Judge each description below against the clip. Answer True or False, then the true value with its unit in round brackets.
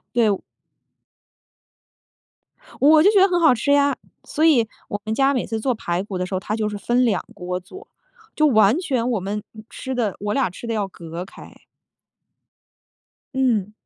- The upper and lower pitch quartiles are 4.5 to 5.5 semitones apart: True (5.2 semitones)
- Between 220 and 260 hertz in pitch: True (225 Hz)